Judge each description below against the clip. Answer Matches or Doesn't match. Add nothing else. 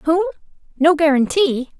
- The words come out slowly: Matches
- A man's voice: Doesn't match